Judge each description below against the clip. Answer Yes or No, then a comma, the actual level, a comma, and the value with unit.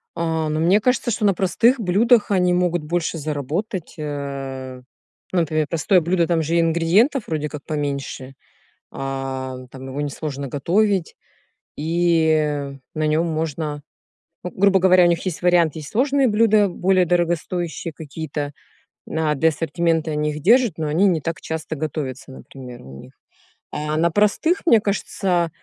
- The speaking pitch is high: No, medium, 165 Hz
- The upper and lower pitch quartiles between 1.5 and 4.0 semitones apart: Yes, average, 3.7 semitones